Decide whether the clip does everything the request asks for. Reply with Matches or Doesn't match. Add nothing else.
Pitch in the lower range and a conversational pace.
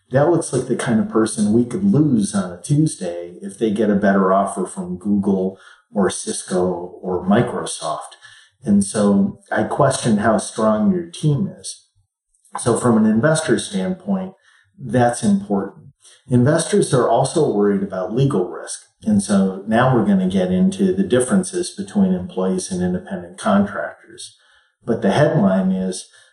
Matches